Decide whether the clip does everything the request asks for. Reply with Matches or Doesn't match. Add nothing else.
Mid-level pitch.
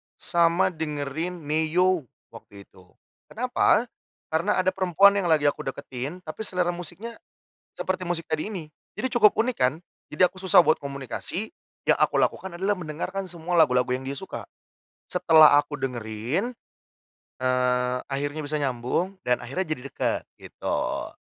Matches